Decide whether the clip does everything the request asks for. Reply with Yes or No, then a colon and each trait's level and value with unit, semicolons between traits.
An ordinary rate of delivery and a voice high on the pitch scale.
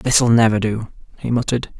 No: average, 165 wpm; low, 115 Hz